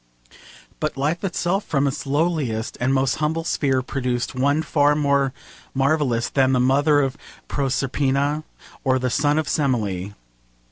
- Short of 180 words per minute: Yes, average, 140 wpm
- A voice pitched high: No, medium, 140 Hz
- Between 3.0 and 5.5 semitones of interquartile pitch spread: No, narrow, 2.5 semitones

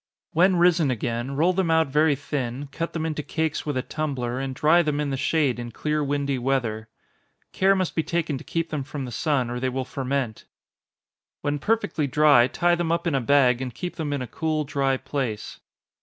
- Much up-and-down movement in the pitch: No, average, 3.6 semitones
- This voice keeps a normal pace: No, fast, 210 wpm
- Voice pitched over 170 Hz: No, medium, 145 Hz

